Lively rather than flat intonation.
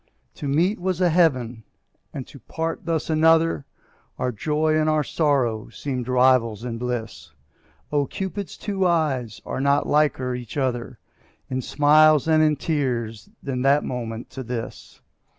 No: average, 4.1 semitones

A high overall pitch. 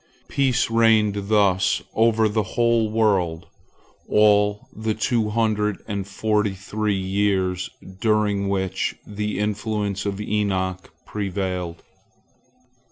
No: low, 105 Hz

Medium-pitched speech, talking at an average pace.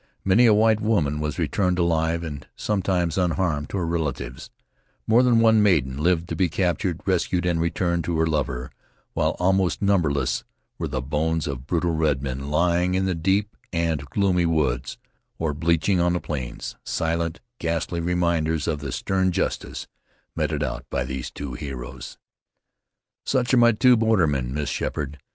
No: very low, 85 Hz; average, 160 wpm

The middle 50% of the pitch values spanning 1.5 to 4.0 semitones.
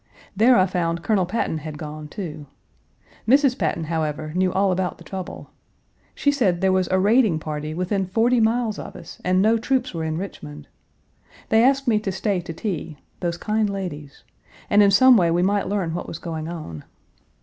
No: average, 4.8 semitones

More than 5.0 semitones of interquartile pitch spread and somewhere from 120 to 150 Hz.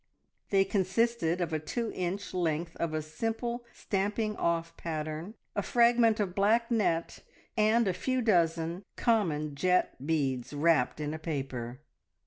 No: wide, 5.6 semitones; medium, 180 Hz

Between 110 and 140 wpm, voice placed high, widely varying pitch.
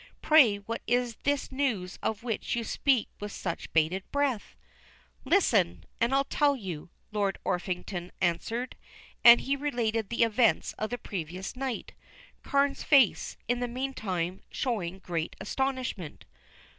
Yes: slow, 135 wpm; high, 225 Hz; wide, 5.8 semitones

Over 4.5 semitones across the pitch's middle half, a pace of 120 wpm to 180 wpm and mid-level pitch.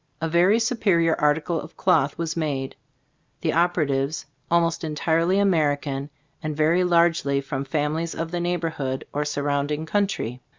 No: average, 2.9 semitones; slow, 135 wpm; medium, 160 Hz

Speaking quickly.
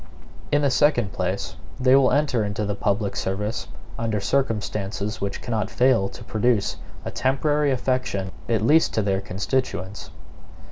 No: average, 145 wpm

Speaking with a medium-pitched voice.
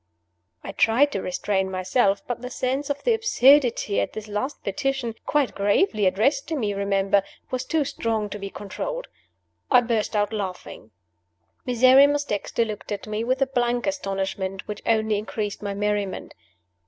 No: high, 220 Hz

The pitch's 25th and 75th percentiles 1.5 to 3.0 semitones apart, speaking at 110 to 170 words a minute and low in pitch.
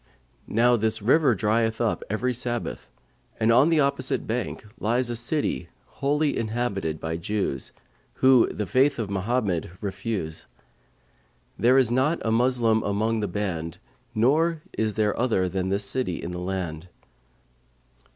No: average, 4.2 semitones; average, 140 wpm; low, 110 Hz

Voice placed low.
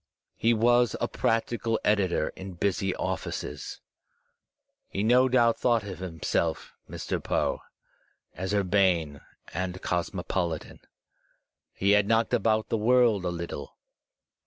Yes: low, 100 Hz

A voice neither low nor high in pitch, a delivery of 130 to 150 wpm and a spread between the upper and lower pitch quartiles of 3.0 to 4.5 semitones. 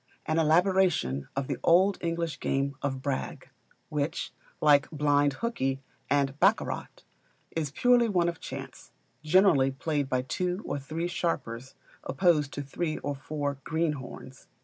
Yes: medium, 150 Hz; slow, 135 wpm; average, 3.8 semitones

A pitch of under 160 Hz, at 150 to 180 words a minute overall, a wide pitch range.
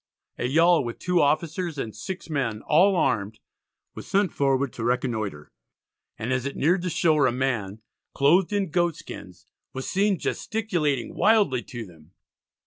Yes: medium, 140 Hz; average, 155 wpm; wide, 6.7 semitones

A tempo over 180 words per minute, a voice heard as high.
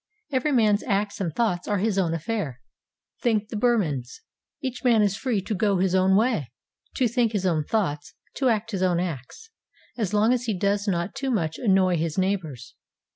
Yes: average, 190 wpm; high, 200 Hz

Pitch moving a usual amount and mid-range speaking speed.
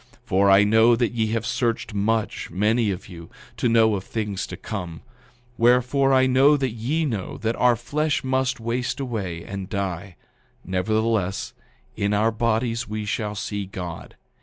Yes: average, 3.4 semitones; average, 165 wpm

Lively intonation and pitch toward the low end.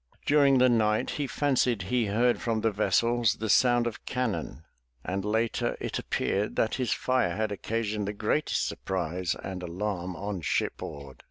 No: average, 4.0 semitones; low, 110 Hz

